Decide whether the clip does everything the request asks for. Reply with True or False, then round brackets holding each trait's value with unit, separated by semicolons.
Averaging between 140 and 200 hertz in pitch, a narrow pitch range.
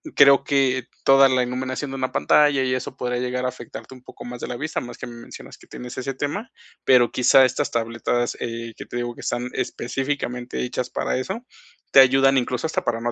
False (125 Hz; 1.8 semitones)